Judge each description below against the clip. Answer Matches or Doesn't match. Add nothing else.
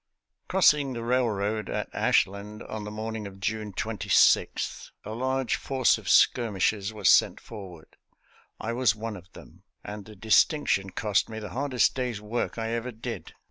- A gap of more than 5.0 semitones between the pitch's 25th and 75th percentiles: Doesn't match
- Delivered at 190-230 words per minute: Doesn't match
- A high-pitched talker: Doesn't match